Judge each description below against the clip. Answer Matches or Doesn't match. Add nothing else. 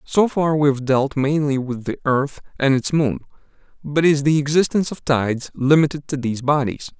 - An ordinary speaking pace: Matches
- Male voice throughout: Matches